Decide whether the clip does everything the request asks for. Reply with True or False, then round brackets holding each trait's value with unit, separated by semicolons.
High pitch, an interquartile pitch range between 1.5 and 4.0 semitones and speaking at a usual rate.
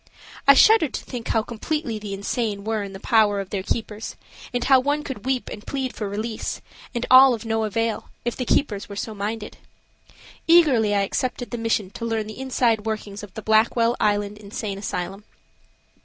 True (220 Hz; 3.1 semitones; 190 wpm)